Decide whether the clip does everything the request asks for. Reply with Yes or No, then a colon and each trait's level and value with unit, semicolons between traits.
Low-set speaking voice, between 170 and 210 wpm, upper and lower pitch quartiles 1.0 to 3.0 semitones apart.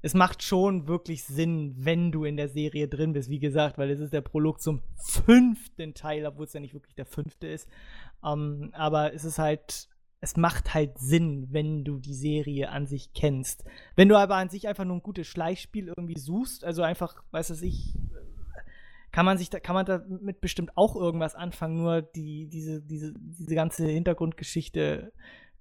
No: medium, 160 Hz; average, 190 wpm; narrow, 2.6 semitones